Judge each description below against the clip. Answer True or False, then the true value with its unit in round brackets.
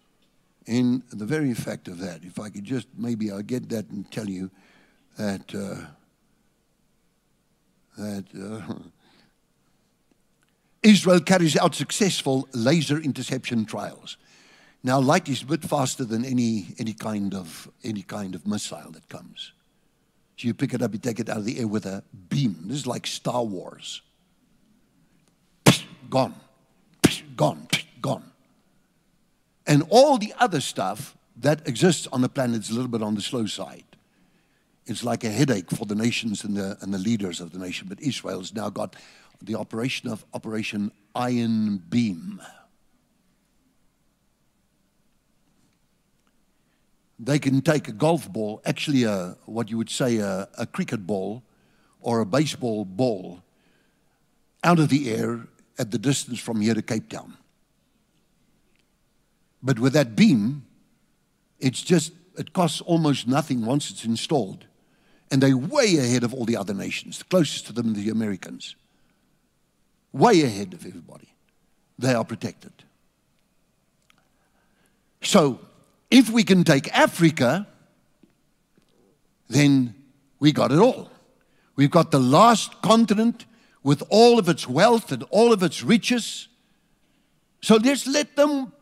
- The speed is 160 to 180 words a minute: False (140 wpm)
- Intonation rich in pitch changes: True (6.4 semitones)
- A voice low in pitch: True (130 Hz)